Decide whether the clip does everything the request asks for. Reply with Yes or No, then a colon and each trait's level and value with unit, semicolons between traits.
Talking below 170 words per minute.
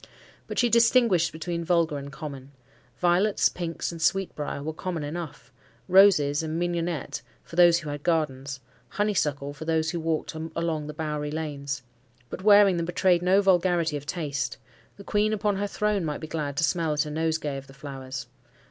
No: average, 175 wpm